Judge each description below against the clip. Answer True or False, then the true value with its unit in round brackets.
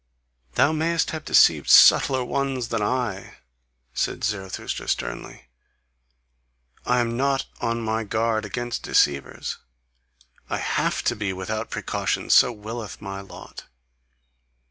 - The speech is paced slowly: True (120 wpm)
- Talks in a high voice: False (115 Hz)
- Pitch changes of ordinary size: True (3.5 semitones)